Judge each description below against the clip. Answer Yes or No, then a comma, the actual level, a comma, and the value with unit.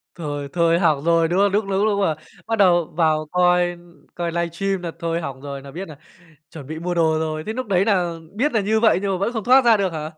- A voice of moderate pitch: Yes, medium, 175 Hz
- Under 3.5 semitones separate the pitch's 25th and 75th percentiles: No, average, 3.8 semitones